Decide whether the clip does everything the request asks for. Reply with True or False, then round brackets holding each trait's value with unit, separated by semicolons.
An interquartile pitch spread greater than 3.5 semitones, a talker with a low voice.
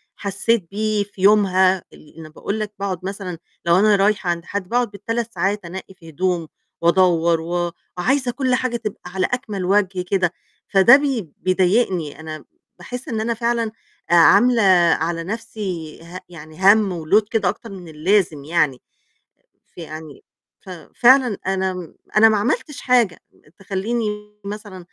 False (3.9 semitones; 195 Hz)